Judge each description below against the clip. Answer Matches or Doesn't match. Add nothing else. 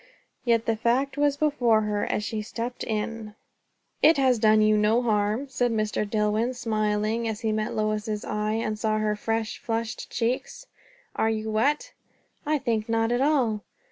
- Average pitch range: Doesn't match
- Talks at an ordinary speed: Matches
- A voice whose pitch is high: Matches